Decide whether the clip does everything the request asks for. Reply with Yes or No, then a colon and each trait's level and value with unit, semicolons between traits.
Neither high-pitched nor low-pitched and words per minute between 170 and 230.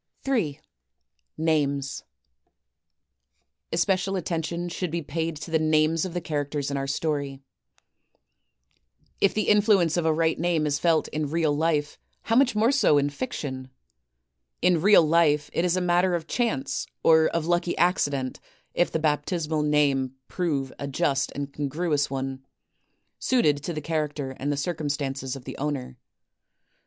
No: medium, 155 Hz; average, 150 wpm